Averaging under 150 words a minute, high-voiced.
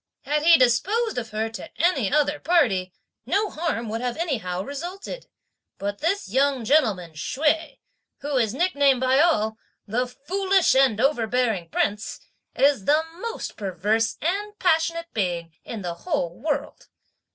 Yes: average, 140 wpm; very high, 270 Hz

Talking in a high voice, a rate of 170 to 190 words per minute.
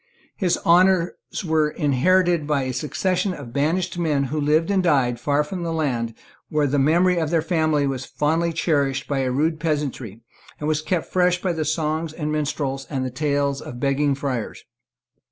No: medium, 150 Hz; average, 180 wpm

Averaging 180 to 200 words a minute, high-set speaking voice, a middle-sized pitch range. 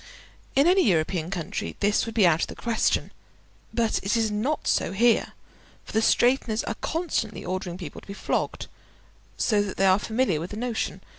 Yes: average, 190 wpm; high, 210 Hz; average, 4.1 semitones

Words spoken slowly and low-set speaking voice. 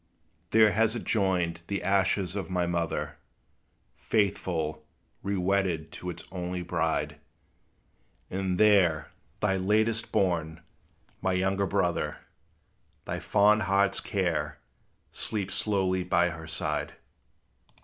Yes: slow, 110 wpm; very low, 95 Hz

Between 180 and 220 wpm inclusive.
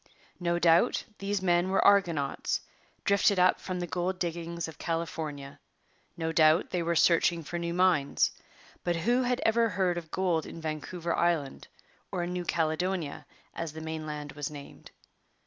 No: average, 160 wpm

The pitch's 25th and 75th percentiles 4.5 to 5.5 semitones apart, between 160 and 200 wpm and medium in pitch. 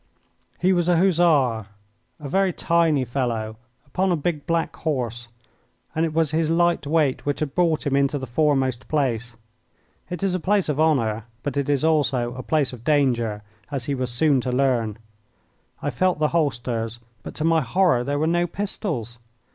Yes: average, 4.9 semitones; average, 180 wpm; medium, 145 Hz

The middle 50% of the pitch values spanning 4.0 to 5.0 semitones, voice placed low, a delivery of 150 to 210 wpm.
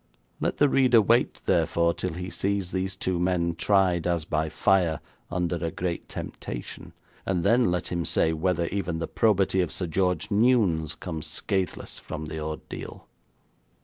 No: average, 2.8 semitones; very low, 90 Hz; average, 160 wpm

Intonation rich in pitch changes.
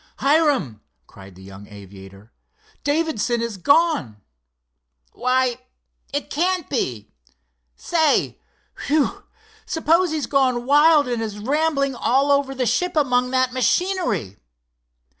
Yes: wide, 6.7 semitones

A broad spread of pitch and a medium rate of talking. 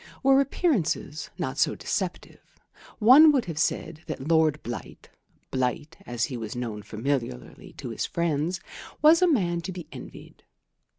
Yes: wide, 8.1 semitones; average, 145 wpm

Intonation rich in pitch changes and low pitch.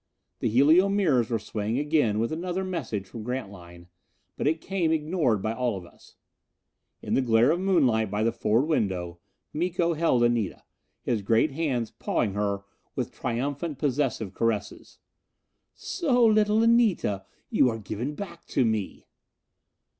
Yes: wide, 7.3 semitones; low, 125 Hz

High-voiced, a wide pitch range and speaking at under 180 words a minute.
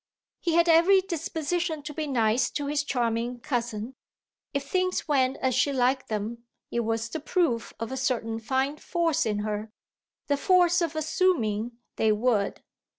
Yes: very high, 265 Hz; wide, 5.9 semitones; average, 160 wpm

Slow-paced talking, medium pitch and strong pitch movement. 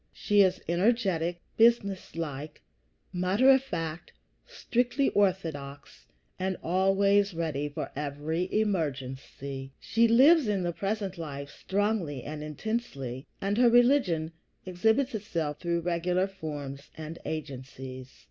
Yes: slow, 110 wpm; medium, 175 Hz; wide, 5.7 semitones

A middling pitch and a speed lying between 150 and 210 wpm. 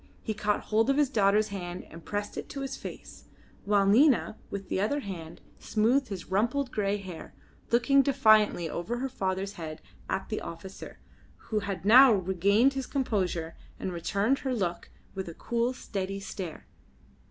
No: high, 205 Hz; average, 165 wpm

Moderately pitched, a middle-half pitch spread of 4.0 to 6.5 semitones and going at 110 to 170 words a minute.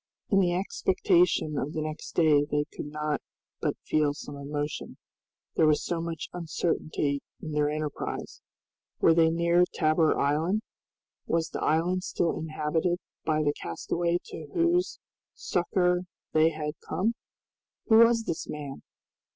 No: medium, 160 Hz; average, 2.7 semitones; average, 140 wpm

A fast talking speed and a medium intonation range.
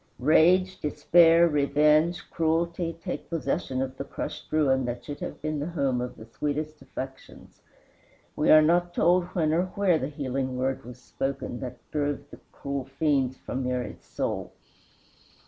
No: average, 155 wpm; average, 3.8 semitones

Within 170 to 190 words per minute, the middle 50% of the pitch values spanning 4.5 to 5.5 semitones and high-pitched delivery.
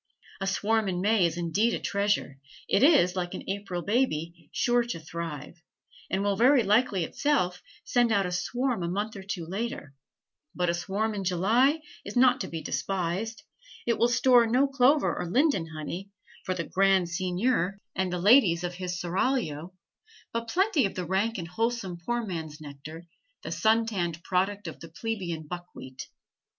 Yes: average, 175 wpm; average, 5.0 semitones; high, 195 Hz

